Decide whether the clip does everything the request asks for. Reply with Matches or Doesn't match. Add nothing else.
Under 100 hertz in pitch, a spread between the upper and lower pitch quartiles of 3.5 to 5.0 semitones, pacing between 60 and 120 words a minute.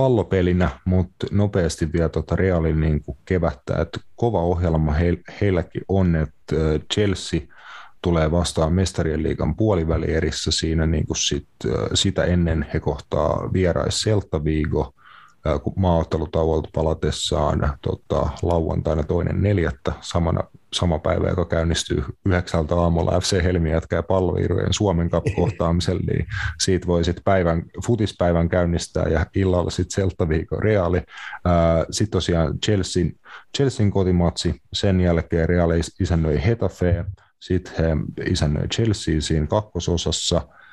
Doesn't match